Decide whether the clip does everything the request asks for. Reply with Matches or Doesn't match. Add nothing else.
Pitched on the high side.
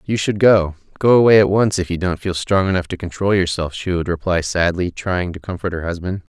Doesn't match